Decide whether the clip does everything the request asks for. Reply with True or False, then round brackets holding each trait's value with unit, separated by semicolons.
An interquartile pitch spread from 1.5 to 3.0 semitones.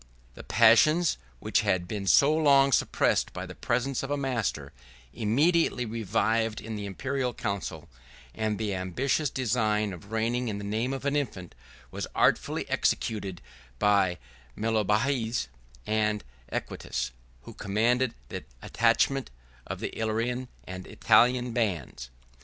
False (3.7 semitones)